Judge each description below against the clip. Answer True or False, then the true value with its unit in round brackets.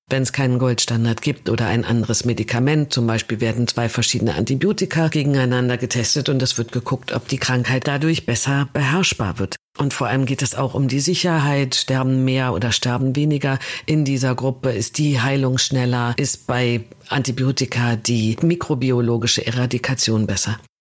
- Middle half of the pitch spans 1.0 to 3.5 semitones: True (2.7 semitones)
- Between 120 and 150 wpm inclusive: False (160 wpm)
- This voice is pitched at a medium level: False (130 Hz)